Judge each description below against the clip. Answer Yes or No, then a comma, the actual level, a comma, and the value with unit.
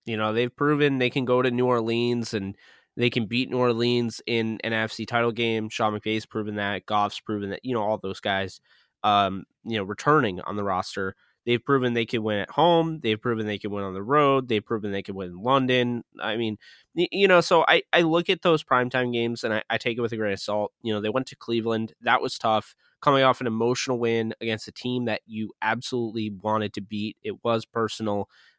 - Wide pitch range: No, average, 2.8 semitones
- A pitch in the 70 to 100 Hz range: No, low, 115 Hz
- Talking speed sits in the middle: No, fast, 230 wpm